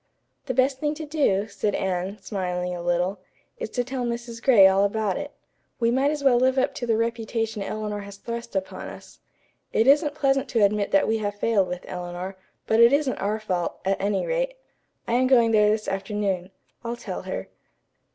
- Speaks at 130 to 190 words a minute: No, average, 200 wpm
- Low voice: No, high, 220 Hz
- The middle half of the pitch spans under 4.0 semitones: No, average, 4.6 semitones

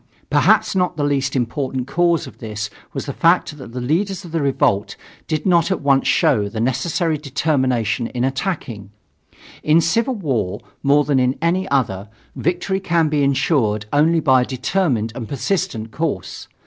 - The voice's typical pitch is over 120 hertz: Yes, medium, 140 Hz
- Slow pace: No, average, 165 wpm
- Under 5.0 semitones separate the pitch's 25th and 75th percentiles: No, average, 5.3 semitones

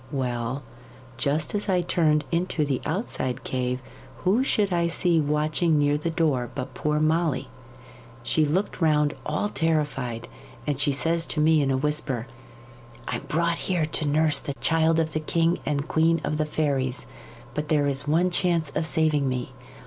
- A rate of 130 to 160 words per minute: No, average, 170 wpm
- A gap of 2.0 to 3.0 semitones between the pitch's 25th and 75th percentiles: Yes, average, 2.7 semitones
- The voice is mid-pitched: Yes, medium, 150 Hz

